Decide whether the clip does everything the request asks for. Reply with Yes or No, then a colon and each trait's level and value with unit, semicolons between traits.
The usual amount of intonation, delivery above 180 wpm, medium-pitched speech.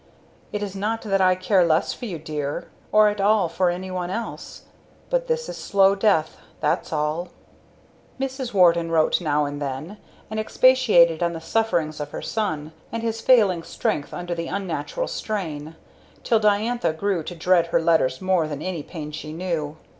No: average, 4.9 semitones; average, 175 wpm; medium, 180 Hz